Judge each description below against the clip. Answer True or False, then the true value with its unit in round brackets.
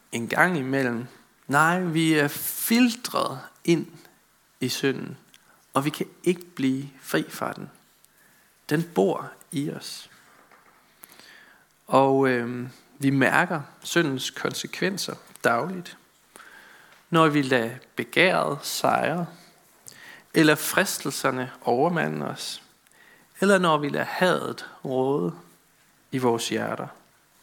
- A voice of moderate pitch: True (145 Hz)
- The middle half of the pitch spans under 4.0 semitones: False (4.6 semitones)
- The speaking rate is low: True (105 wpm)